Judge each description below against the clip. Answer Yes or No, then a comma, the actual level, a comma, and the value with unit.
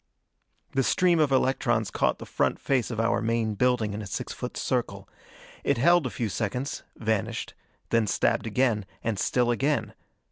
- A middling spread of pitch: Yes, average, 3.4 semitones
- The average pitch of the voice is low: Yes, low, 120 Hz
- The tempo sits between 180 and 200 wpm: No, average, 170 wpm